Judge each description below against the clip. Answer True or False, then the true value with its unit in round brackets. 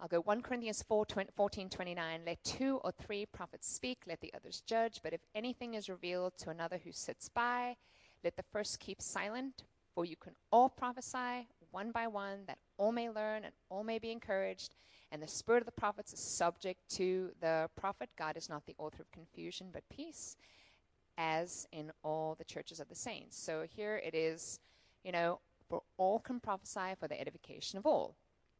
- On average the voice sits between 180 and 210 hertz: True (185 Hz)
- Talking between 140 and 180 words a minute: False (195 wpm)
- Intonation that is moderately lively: True (5.0 semitones)